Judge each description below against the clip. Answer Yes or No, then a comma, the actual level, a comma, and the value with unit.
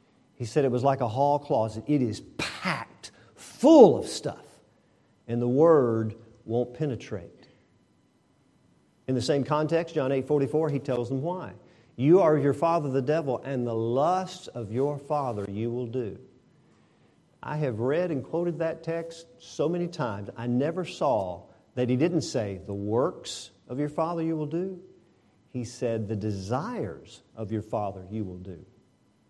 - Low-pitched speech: Yes, low, 130 Hz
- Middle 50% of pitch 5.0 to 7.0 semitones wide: Yes, wide, 5.4 semitones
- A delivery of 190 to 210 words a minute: No, average, 165 wpm